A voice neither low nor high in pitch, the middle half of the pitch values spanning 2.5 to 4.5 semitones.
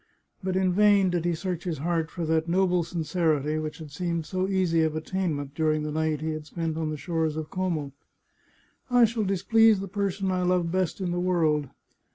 Yes: medium, 170 Hz; average, 3.0 semitones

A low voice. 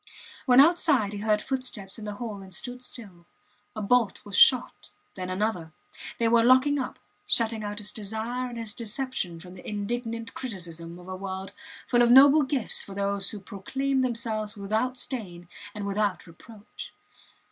No: high, 215 Hz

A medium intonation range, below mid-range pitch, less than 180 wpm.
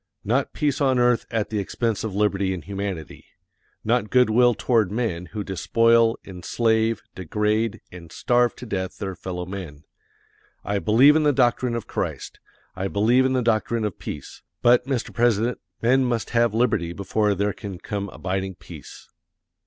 Yes: average, 3.7 semitones; low, 110 Hz; average, 165 wpm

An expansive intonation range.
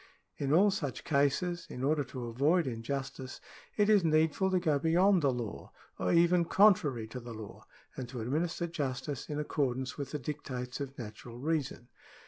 No: average, 4.8 semitones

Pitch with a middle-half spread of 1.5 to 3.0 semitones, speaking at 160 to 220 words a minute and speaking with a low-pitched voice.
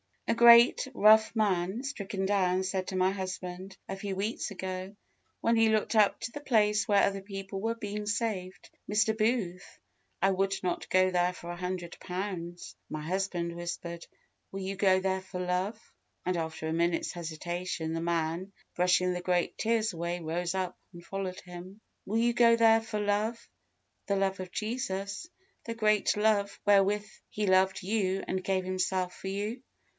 No: average, 2.7 semitones; average, 170 wpm; high, 190 Hz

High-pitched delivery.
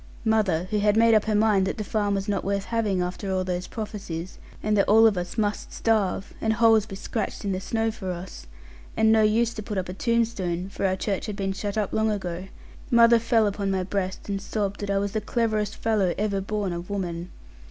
Yes: high, 205 Hz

